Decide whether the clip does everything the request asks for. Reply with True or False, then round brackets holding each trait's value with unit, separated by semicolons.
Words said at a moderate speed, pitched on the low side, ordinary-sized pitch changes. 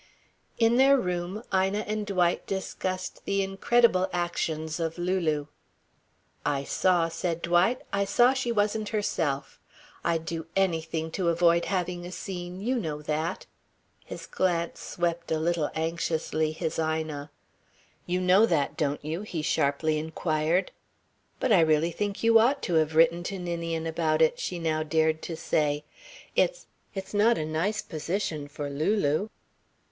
False (150 wpm; 170 Hz; 3.4 semitones)